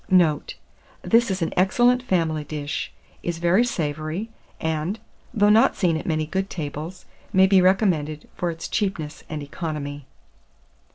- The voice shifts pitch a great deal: No, average, 3.7 semitones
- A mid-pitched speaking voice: Yes, medium, 170 Hz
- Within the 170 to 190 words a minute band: No, average, 145 wpm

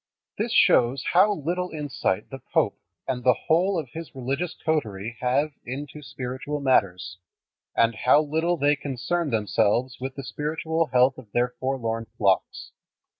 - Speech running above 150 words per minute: No, average, 145 wpm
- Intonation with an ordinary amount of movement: Yes, average, 4.2 semitones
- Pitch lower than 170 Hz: Yes, low, 135 Hz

